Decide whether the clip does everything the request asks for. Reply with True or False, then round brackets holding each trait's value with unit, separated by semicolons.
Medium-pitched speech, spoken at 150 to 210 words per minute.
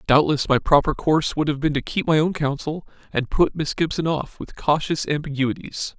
True (150 Hz; 200 wpm)